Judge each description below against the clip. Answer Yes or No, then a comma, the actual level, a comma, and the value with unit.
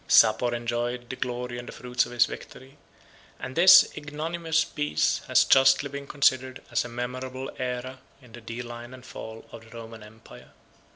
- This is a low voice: Yes, low, 125 Hz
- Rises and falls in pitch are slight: Yes, narrow, 1.9 semitones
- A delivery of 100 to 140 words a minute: No, average, 170 wpm